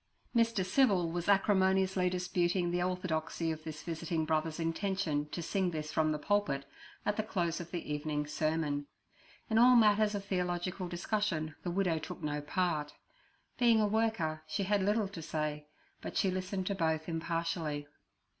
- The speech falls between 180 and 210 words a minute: No, average, 165 wpm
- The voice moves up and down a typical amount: Yes, average, 3.8 semitones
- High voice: No, medium, 175 Hz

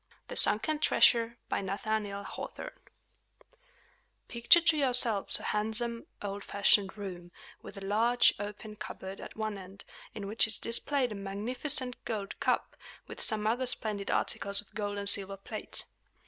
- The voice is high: Yes, high, 215 Hz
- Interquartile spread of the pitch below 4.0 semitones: Yes, average, 2.8 semitones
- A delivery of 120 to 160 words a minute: Yes, average, 150 wpm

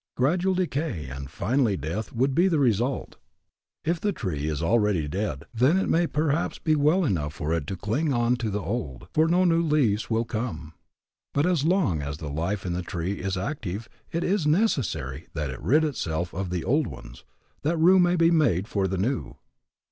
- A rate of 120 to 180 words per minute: No, average, 200 wpm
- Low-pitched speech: Yes, low, 115 Hz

